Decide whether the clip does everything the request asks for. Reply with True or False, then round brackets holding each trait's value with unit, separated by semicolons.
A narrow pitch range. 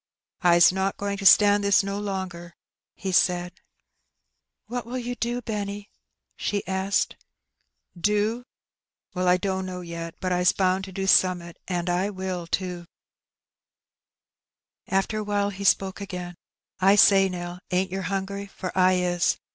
True (1.9 semitones)